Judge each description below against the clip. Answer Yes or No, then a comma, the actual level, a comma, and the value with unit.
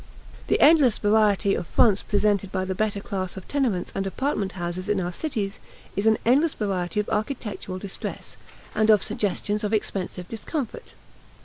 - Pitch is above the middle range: Yes, high, 205 Hz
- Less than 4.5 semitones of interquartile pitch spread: Yes, narrow, 2.5 semitones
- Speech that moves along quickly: No, average, 165 wpm